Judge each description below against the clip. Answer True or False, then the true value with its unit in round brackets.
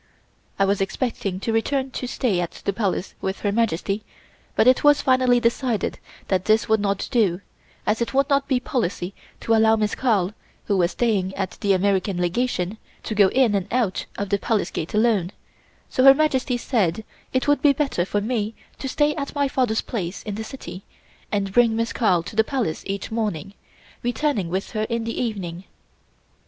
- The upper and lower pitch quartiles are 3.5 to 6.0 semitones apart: True (4.2 semitones)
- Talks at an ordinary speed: True (190 wpm)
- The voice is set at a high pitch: True (220 Hz)